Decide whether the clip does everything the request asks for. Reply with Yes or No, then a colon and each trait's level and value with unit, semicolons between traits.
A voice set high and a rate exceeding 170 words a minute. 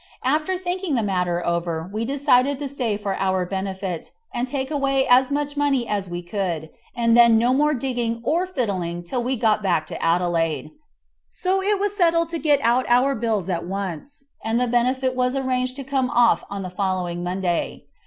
Yes: high, 240 Hz; average, 190 wpm